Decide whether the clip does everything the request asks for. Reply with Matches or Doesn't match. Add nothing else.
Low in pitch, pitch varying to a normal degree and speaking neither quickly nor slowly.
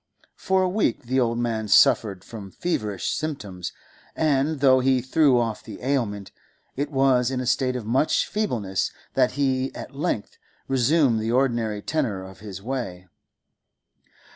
Matches